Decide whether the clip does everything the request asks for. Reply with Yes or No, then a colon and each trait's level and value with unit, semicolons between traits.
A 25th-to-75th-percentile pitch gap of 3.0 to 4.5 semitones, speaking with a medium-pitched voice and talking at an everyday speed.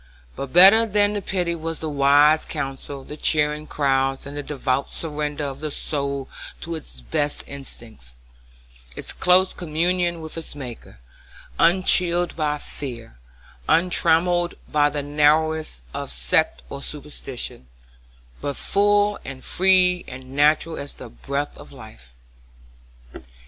No: average, 3.8 semitones; medium, 150 Hz; slow, 130 wpm